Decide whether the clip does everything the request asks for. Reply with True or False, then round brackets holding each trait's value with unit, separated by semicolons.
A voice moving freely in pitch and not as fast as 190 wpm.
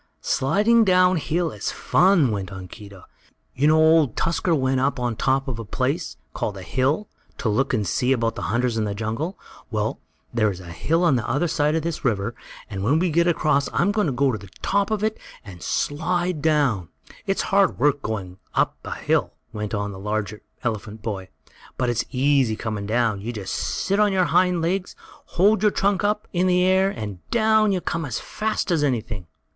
False (8.6 semitones; 200 wpm)